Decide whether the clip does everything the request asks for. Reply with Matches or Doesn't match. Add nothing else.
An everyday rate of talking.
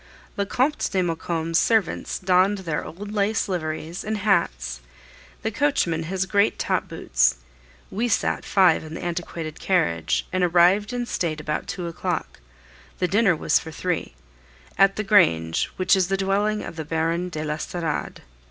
Matches